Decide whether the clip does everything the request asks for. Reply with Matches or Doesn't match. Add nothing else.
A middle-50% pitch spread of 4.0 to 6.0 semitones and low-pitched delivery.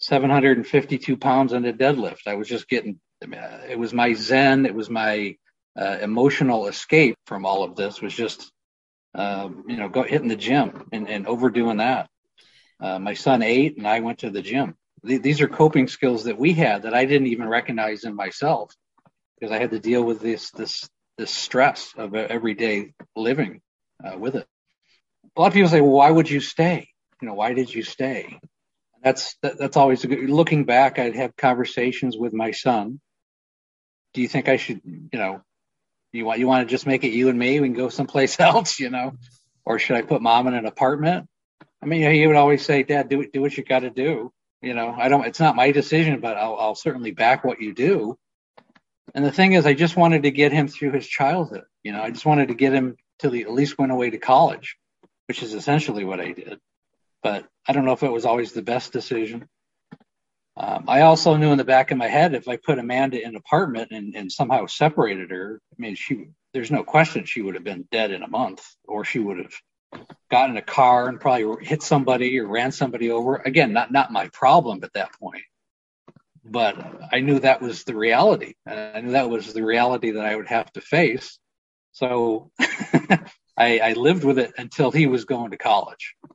Doesn't match